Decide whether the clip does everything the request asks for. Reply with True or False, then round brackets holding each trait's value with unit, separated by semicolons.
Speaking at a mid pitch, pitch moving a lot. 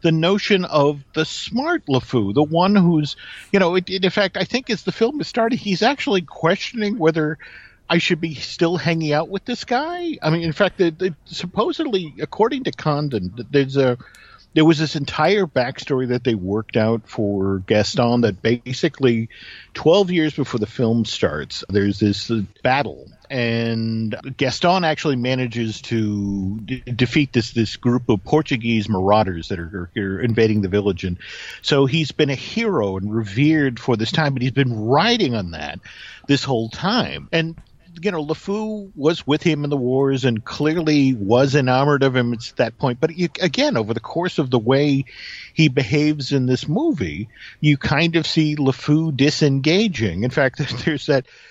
True (145 Hz; 6.1 semitones)